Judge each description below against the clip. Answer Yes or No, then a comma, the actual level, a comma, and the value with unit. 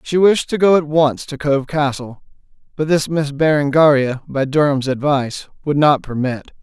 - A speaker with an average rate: Yes, average, 170 wpm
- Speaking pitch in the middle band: Yes, medium, 145 Hz